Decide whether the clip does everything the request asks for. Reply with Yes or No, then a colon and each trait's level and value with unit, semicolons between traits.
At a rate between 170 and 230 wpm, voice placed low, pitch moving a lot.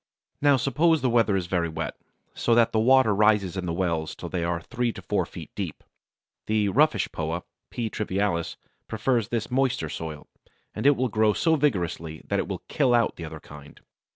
Yes: average, 195 wpm; low, 110 Hz; wide, 6.4 semitones